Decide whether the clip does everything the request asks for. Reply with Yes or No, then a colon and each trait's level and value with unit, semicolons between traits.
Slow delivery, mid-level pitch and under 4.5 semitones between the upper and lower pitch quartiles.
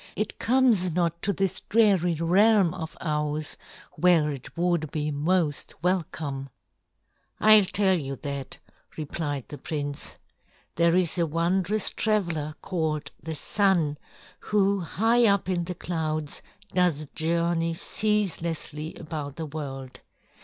Yes: slow, 125 wpm; medium, 170 Hz; average, 3.7 semitones